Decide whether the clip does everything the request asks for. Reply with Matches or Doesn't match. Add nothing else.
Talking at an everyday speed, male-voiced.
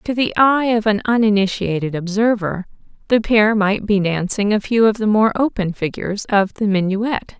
Doesn't match